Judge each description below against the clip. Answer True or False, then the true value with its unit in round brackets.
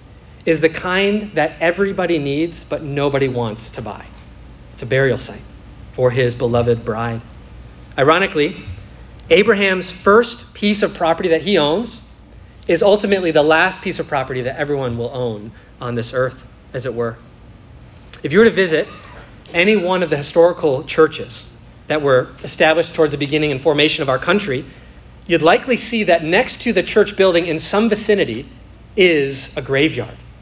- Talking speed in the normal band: True (160 wpm)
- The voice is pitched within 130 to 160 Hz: True (155 Hz)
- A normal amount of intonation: False (6.5 semitones)